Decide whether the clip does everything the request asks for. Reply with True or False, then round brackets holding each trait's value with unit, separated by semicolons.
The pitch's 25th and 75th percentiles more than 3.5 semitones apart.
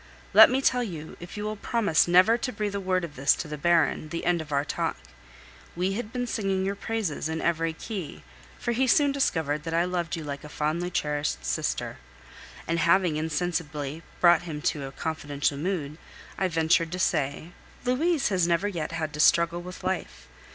True (4.2 semitones)